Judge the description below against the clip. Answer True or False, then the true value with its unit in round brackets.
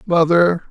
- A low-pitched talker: False (170 Hz)